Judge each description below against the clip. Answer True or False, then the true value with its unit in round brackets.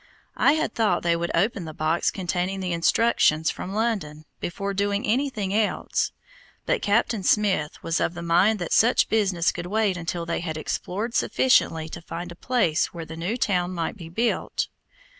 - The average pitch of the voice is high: False (180 Hz)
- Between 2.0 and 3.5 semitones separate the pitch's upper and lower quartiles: False (4.2 semitones)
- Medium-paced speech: True (180 wpm)